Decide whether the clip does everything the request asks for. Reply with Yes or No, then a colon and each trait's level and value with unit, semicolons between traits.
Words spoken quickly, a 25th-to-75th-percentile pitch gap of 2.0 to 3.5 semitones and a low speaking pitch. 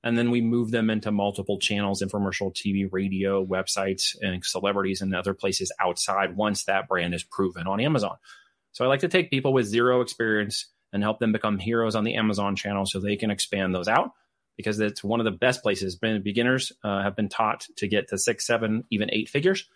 Yes: fast, 215 wpm; average, 2.9 semitones; low, 105 Hz